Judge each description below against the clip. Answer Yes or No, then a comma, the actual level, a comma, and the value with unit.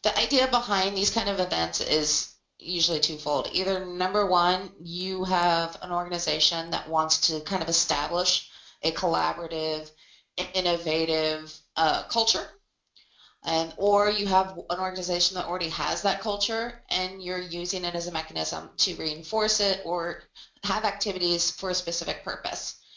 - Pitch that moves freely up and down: No, average, 2.9 semitones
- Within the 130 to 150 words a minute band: Yes, average, 145 wpm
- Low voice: No, medium, 175 Hz